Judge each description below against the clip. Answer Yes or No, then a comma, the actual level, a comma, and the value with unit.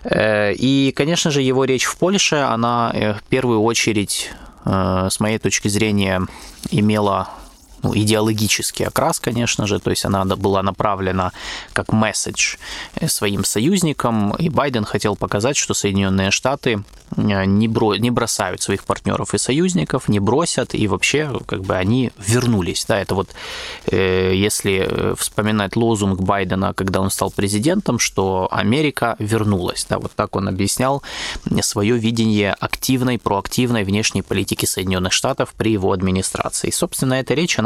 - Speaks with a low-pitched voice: Yes, low, 105 Hz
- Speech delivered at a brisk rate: No, average, 140 wpm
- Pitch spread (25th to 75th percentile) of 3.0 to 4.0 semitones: Yes, average, 3.7 semitones